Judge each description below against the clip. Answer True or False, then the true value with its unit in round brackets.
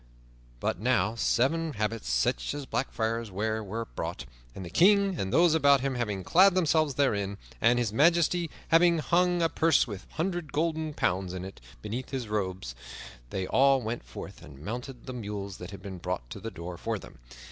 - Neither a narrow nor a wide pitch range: False (8.0 semitones)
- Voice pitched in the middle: False (120 Hz)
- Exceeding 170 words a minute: True (190 wpm)